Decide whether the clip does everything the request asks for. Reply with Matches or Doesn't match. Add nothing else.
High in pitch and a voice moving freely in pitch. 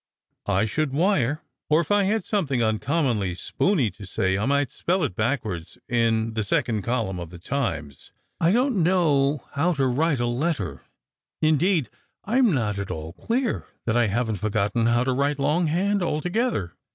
Doesn't match